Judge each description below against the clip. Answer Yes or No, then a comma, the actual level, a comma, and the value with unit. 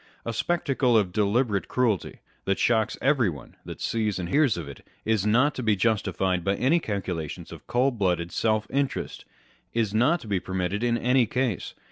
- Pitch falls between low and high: No, low, 110 Hz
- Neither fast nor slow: Yes, average, 175 wpm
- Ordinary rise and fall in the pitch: Yes, average, 4.5 semitones